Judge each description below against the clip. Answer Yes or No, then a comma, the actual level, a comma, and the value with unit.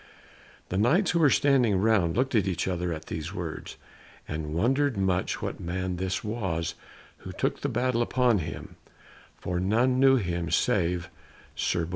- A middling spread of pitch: No, wide, 6.2 semitones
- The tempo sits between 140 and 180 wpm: Yes, average, 165 wpm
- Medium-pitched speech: No, very low, 95 Hz